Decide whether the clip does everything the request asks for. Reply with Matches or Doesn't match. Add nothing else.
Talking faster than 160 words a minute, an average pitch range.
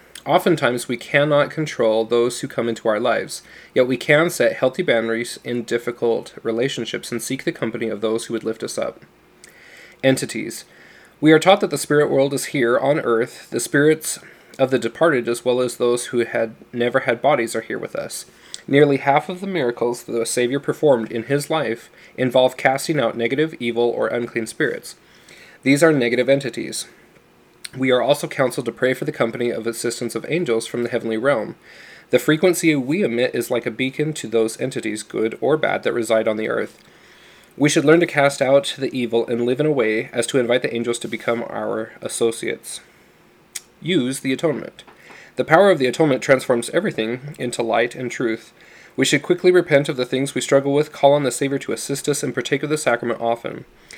Matches